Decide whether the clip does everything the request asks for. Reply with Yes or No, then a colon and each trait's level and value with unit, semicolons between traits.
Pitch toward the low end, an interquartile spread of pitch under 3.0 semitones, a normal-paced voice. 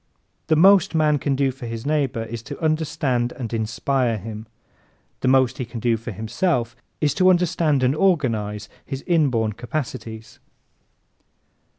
No: low, 130 Hz; average, 5.1 semitones; average, 150 wpm